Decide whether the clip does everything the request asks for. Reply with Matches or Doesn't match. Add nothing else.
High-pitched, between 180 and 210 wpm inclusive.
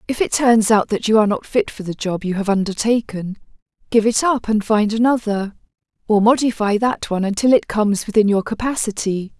Matches